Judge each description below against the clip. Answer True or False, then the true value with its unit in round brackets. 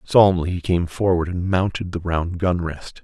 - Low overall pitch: True (90 Hz)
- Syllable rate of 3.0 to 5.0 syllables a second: True (4.8 syllables/s)